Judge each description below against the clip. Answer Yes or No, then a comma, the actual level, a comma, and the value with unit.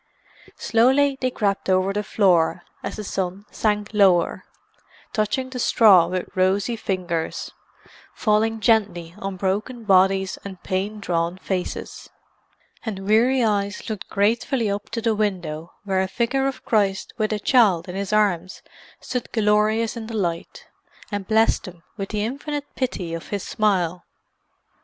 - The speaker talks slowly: No, average, 145 wpm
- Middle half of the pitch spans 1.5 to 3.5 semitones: Yes, average, 3.0 semitones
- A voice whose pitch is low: No, high, 205 Hz